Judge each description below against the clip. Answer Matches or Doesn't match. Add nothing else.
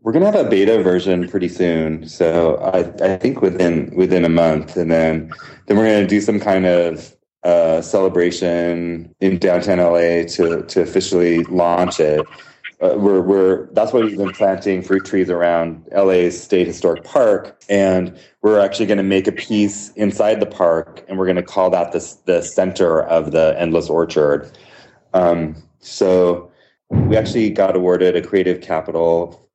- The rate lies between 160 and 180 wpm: Matches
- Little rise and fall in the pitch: Matches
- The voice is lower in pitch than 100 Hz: Matches